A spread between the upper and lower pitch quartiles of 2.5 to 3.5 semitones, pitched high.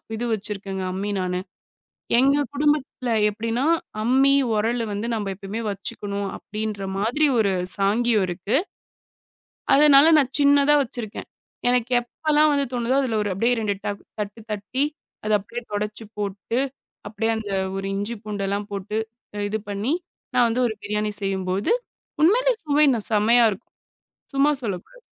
No: average, 4.0 semitones; high, 220 Hz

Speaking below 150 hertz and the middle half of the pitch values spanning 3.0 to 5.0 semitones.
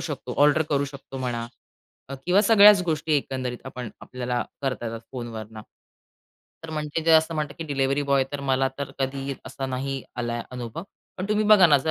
Yes: low, 135 Hz; average, 3.7 semitones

